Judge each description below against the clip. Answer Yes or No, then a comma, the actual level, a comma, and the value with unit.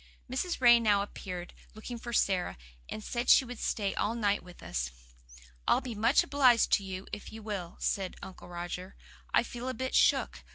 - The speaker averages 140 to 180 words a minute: No, average, 190 wpm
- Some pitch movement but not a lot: Yes, average, 4.2 semitones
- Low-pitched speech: No, high, 215 Hz